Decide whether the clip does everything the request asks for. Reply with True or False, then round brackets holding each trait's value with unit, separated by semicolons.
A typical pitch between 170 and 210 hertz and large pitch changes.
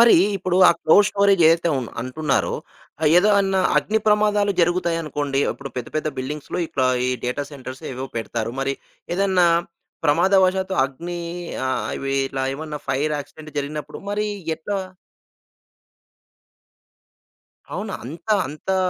False (155 Hz; 5.7 semitones)